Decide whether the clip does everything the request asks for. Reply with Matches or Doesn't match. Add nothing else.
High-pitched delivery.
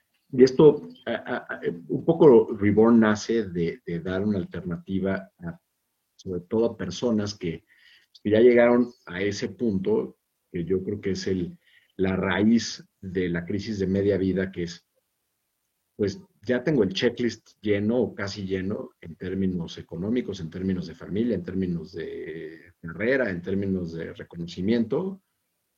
Doesn't match